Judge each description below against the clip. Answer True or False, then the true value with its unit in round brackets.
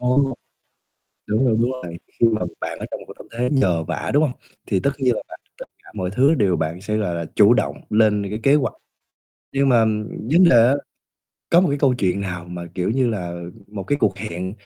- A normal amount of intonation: False (5.8 semitones)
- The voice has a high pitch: False (110 Hz)